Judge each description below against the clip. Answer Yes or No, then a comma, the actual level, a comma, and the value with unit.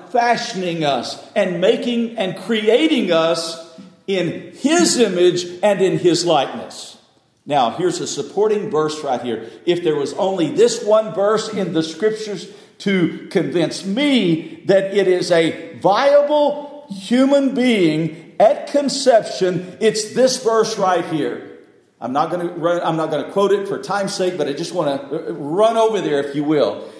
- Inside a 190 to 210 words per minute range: No, average, 160 wpm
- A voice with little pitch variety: No, average, 5.1 semitones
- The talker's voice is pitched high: Yes, high, 195 Hz